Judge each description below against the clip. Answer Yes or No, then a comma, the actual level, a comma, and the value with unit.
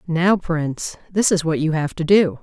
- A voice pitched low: No, medium, 165 Hz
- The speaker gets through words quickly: Yes, fast, 225 wpm